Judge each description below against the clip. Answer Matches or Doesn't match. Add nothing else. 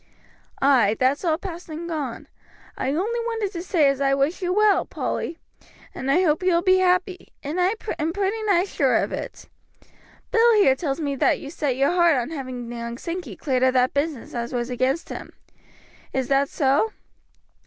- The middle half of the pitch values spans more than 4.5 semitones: Matches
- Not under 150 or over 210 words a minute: Matches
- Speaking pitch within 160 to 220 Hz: Doesn't match